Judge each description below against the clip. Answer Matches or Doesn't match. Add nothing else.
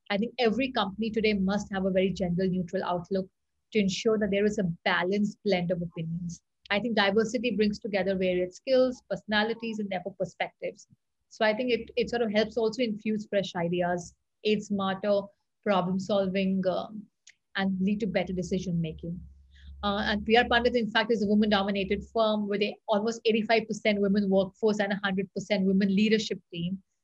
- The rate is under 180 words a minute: Matches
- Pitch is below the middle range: Doesn't match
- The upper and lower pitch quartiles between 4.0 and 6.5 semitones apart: Doesn't match